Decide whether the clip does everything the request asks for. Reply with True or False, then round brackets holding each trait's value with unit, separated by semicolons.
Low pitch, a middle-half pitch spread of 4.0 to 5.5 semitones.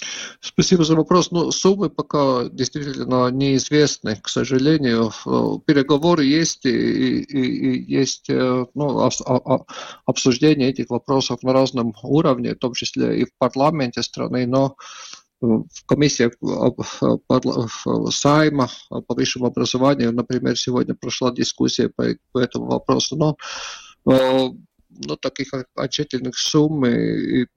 False (130 Hz; 2.9 semitones)